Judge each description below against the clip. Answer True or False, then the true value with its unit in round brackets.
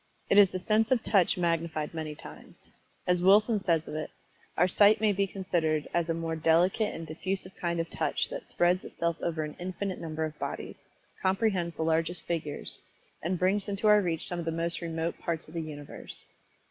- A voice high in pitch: False (170 Hz)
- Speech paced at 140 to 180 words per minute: False (200 wpm)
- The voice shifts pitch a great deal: False (2.9 semitones)